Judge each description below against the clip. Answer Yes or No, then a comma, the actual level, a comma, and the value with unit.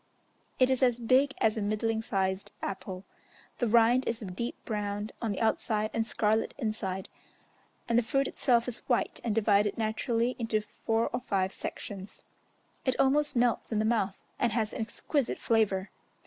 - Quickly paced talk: No, average, 170 wpm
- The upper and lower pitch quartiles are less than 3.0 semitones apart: Yes, narrow, 2.5 semitones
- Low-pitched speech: No, high, 225 Hz